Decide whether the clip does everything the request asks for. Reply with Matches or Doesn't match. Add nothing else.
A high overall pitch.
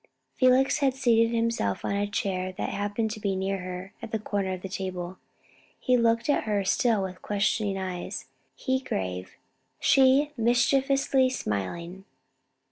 Matches